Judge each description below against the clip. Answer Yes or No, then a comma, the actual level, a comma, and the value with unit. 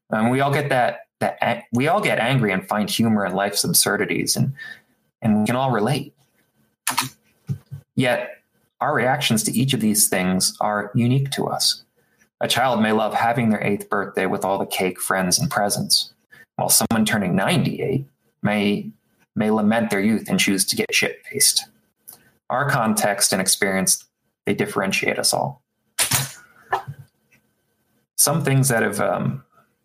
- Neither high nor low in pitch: No, low, 115 Hz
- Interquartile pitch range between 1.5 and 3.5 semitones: No, average, 4.6 semitones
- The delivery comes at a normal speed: Yes, average, 155 wpm